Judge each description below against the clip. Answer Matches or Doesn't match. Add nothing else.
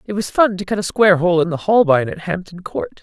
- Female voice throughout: Matches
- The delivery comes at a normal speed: Doesn't match